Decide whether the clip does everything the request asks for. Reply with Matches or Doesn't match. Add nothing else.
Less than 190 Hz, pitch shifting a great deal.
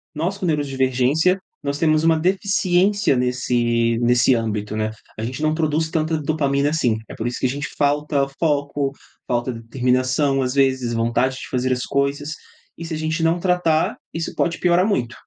Doesn't match